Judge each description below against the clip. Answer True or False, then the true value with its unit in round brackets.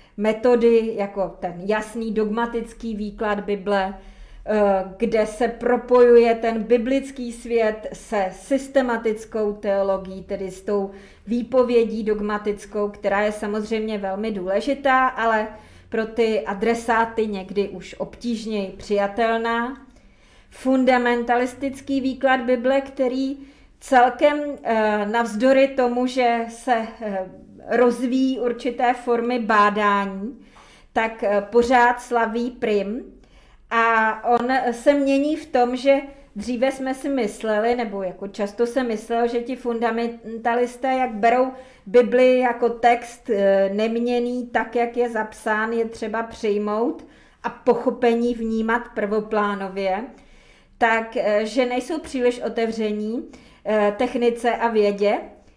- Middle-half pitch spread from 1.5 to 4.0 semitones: True (2.6 semitones)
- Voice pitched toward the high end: True (230 Hz)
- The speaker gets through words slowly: True (100 wpm)